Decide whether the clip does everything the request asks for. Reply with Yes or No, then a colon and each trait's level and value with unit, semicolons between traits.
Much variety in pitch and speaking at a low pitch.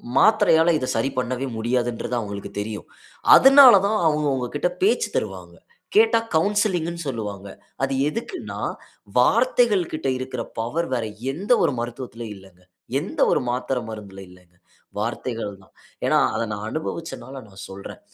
Yes: wide, 7.4 semitones; low, 130 Hz